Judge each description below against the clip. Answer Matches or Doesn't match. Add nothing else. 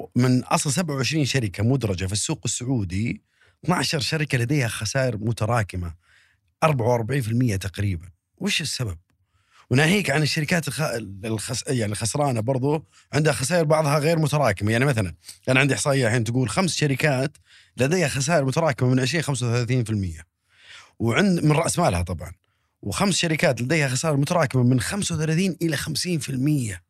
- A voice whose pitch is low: Matches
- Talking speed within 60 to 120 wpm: Doesn't match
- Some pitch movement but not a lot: Doesn't match